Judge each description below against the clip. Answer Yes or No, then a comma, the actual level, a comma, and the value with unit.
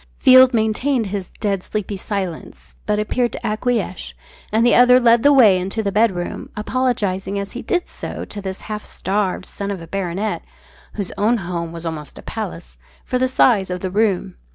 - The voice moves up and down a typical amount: Yes, average, 3.9 semitones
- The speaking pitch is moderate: No, high, 205 Hz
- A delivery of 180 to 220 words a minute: Yes, average, 185 wpm